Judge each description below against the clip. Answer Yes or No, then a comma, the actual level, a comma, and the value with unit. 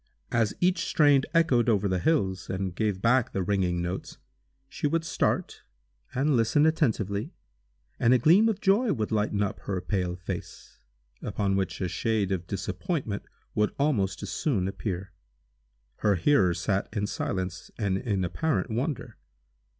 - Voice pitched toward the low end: Yes, low, 105 Hz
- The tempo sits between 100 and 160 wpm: Yes, average, 150 wpm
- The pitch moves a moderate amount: No, wide, 6.5 semitones